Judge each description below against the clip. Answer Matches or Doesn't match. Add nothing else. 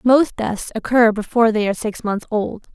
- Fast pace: Doesn't match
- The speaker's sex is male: Doesn't match